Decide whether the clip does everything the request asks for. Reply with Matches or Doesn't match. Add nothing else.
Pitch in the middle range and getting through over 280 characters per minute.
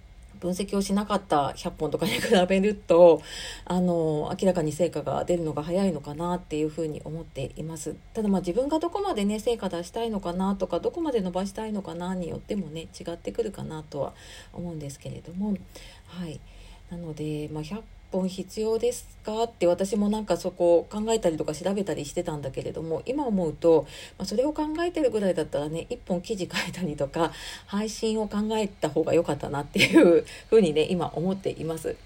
Matches